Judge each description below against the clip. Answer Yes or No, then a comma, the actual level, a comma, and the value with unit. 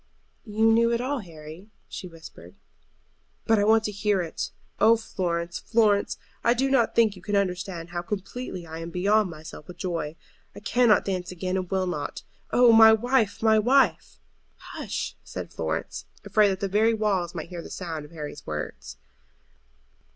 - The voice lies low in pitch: No, high, 195 Hz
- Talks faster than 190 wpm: No, average, 175 wpm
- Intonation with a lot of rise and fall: No, average, 4.4 semitones